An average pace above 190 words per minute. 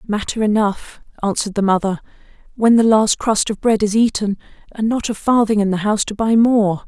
Yes: average, 200 wpm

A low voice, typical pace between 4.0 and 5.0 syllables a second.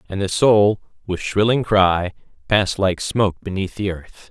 Yes: low, 100 Hz; 4.5 syllables/s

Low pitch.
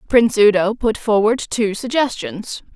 No: high, 215 Hz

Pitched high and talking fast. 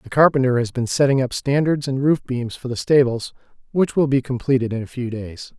No: low, 130 Hz; fast, 225 wpm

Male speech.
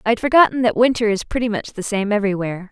No: female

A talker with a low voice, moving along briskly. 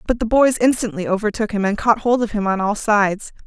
No: high, 215 Hz; fast, 240 wpm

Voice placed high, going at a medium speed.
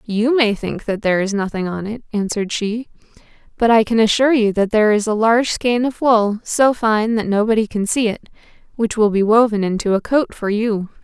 No: high, 220 Hz; fast, 215 wpm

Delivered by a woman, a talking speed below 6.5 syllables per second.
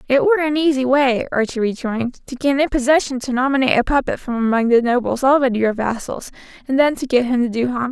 No: female; 6.6 syllables/s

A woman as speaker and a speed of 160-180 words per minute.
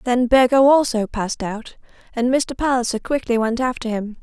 Yes: female; average, 170 wpm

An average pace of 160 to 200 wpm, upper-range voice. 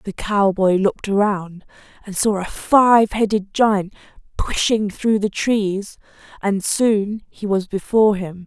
No: average, 140 wpm; high, 205 Hz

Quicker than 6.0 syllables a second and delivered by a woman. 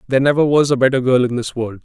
No: 7.2 syllables/s; male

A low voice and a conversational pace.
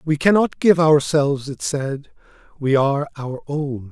No: medium, 145 Hz; average, 155 wpm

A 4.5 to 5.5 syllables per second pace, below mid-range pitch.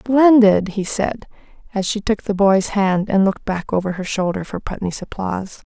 No: 4.8 syllables/s; high, 200 Hz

